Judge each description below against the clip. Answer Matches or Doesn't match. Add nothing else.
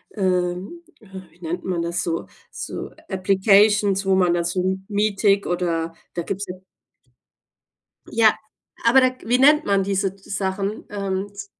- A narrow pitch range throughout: Matches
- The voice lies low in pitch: Doesn't match